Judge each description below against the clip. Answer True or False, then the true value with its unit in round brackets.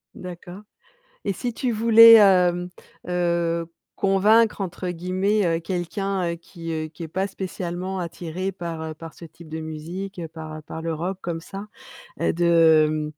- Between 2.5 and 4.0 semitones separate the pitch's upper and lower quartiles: True (2.8 semitones)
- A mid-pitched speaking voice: True (175 Hz)